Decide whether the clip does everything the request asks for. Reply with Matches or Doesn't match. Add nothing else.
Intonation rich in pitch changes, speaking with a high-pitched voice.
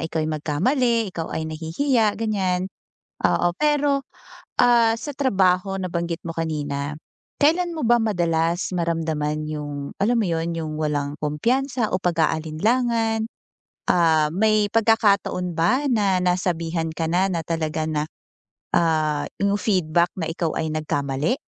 Doesn't match